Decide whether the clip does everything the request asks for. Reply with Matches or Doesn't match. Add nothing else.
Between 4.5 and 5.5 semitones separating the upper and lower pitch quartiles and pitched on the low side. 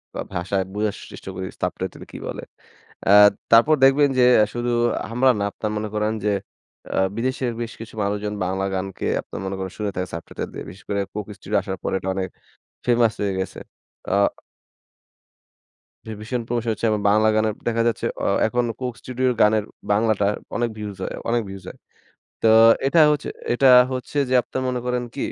Doesn't match